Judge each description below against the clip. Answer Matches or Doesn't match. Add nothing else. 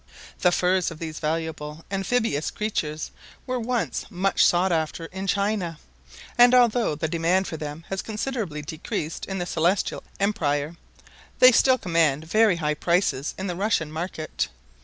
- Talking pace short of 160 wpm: Matches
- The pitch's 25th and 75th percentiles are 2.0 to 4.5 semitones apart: Matches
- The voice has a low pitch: Doesn't match